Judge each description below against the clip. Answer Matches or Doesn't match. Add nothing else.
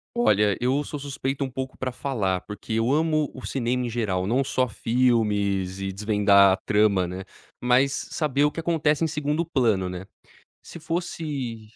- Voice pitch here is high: Doesn't match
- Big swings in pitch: Matches